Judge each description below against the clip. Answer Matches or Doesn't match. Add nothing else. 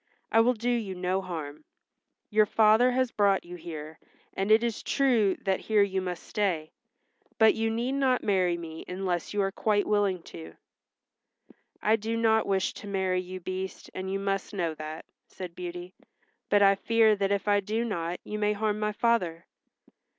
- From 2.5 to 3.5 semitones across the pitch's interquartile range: Matches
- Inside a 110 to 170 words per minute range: Doesn't match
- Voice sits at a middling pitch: Doesn't match